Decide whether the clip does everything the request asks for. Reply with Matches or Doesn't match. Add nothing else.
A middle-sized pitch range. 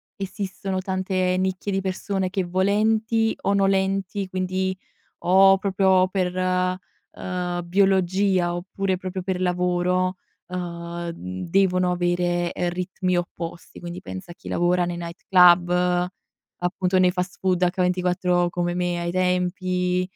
Doesn't match